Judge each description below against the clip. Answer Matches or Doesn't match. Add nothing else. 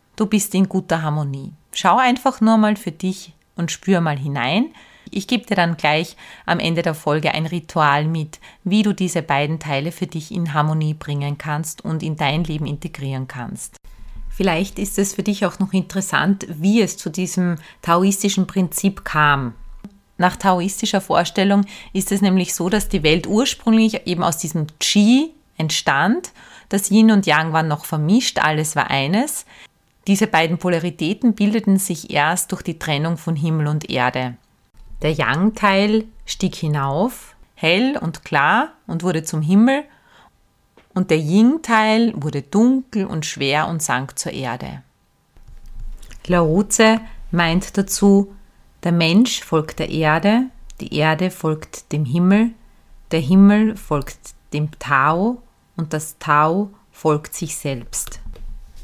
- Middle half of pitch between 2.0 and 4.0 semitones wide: Doesn't match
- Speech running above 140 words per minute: Matches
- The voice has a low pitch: Doesn't match